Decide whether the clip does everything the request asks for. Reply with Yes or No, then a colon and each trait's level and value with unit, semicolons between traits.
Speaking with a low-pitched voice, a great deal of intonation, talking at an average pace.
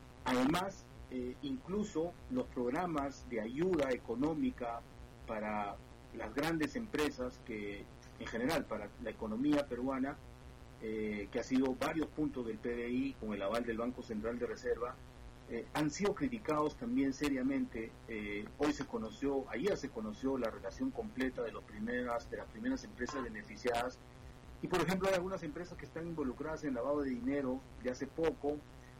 No: low, 130 Hz; average, 4.1 semitones; average, 155 wpm